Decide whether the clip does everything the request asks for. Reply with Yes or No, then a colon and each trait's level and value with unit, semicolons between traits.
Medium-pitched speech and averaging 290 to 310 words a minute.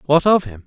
No: medium, 150 Hz; fast, 270 wpm